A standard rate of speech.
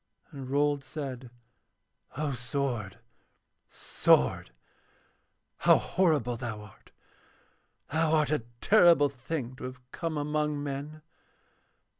No: slow, 100 wpm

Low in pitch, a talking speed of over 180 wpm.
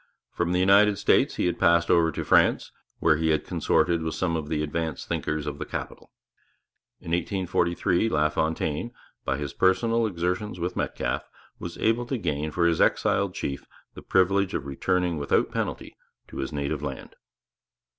No: very low, 85 Hz; average, 165 wpm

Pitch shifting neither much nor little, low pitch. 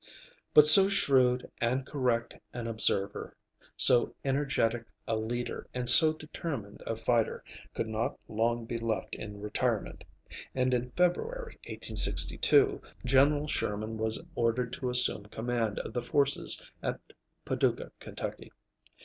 Yes: average, 3.6 semitones; low, 120 Hz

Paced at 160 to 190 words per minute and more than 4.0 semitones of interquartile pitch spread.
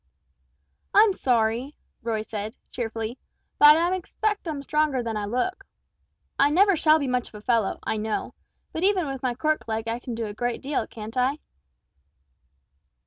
Yes: average, 170 wpm; wide, 5.5 semitones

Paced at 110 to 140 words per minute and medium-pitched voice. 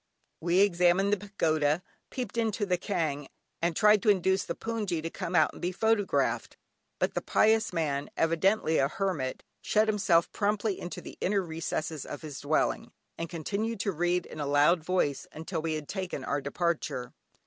No: average, 175 wpm; medium, 175 Hz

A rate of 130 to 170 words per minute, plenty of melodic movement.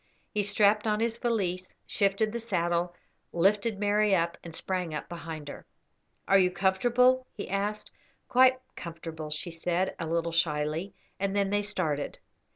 No: average, 155 wpm; average, 3.9 semitones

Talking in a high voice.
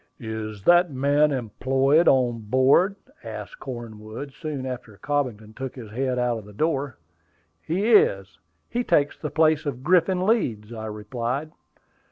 No: low, 130 Hz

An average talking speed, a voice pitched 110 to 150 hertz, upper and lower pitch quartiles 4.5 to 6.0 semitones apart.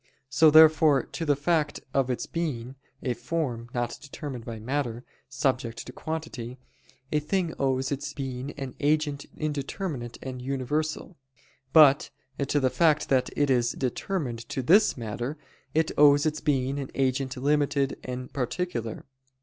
No: average, 145 wpm; medium, 140 Hz; average, 3.2 semitones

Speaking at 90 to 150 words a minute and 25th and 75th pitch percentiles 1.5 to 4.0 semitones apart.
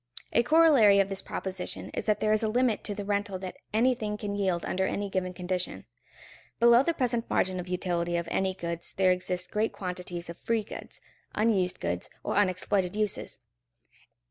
No: average, 180 wpm; average, 2.9 semitones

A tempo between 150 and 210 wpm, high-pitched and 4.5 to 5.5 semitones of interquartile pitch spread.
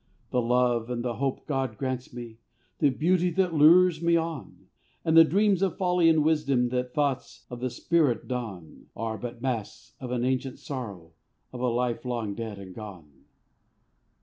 No: average, 175 wpm; low, 125 Hz; average, 5.1 semitones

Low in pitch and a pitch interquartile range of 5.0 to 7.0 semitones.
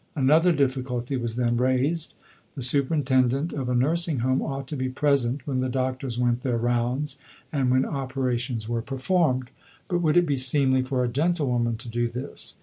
No: low, 130 Hz; narrow, 2.4 semitones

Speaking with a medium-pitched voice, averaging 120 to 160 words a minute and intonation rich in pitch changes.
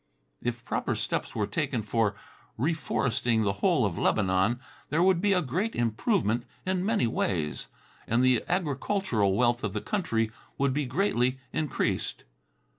No: low, 125 Hz; average, 145 wpm; wide, 7.6 semitones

